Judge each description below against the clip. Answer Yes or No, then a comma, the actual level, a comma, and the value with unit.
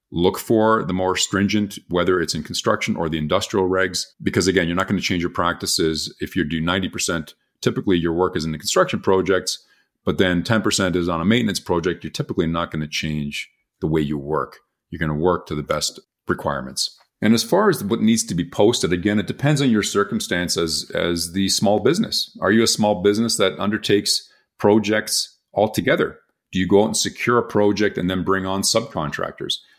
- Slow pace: No, fast, 205 wpm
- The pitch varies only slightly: No, average, 3.6 semitones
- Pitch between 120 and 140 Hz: No, very low, 95 Hz